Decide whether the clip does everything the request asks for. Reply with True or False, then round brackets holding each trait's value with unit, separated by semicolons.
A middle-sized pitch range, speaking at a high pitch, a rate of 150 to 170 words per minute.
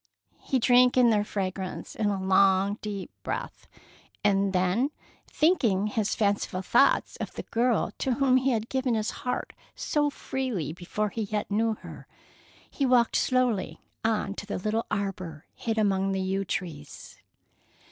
True (4.1 semitones; 210 Hz; 155 wpm)